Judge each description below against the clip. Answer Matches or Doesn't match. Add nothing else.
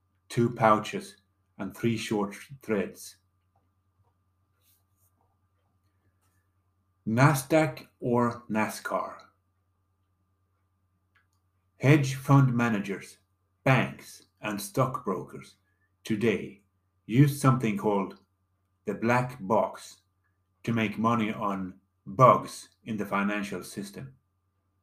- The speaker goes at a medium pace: Doesn't match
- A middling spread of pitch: Matches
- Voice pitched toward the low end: Matches